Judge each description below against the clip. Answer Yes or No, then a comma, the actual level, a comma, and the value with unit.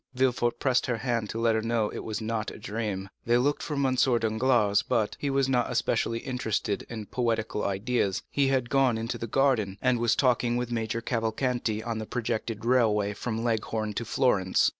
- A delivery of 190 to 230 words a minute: Yes, average, 195 wpm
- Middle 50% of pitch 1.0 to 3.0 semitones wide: Yes, narrow, 2.4 semitones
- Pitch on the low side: Yes, low, 115 Hz